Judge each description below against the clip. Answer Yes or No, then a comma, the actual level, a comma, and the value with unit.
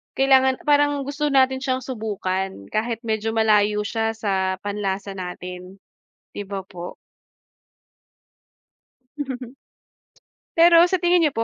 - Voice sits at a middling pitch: No, high, 220 Hz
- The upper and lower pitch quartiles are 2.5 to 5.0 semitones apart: No, wide, 5.4 semitones